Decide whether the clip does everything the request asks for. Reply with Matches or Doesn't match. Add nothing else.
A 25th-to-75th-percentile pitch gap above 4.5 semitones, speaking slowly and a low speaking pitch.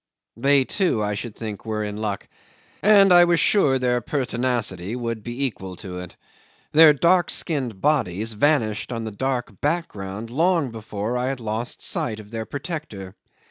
Doesn't match